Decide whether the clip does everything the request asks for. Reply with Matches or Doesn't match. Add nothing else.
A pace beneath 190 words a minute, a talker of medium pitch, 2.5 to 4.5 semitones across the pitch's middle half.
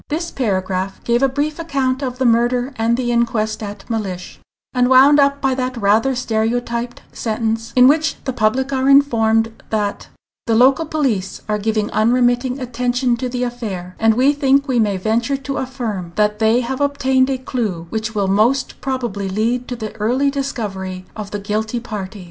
Doesn't match